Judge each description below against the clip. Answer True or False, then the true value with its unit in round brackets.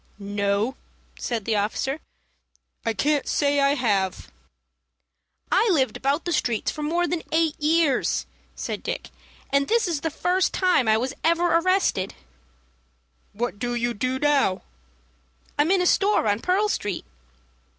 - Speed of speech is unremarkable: True (145 wpm)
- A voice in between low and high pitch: False (280 Hz)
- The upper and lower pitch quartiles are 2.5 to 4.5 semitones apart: False (7.0 semitones)